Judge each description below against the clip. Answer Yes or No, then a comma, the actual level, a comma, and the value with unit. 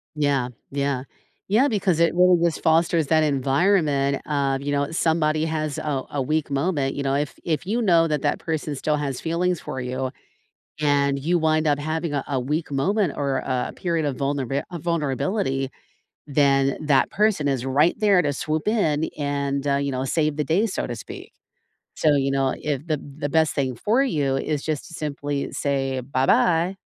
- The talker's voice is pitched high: No, medium, 145 Hz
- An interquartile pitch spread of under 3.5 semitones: Yes, average, 2.9 semitones